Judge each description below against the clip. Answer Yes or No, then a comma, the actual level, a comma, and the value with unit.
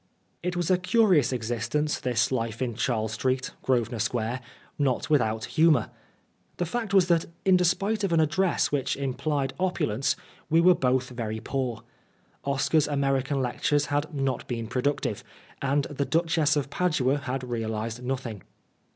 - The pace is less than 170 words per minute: Yes, average, 150 wpm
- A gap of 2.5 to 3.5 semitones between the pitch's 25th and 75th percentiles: No, average, 4.5 semitones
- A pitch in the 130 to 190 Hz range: Yes, low, 135 Hz